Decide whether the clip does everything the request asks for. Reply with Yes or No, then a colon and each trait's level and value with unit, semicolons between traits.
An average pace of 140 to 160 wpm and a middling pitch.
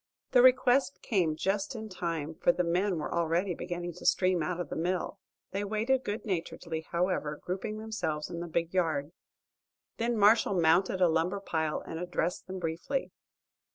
No: average, 170 wpm; medium, 180 Hz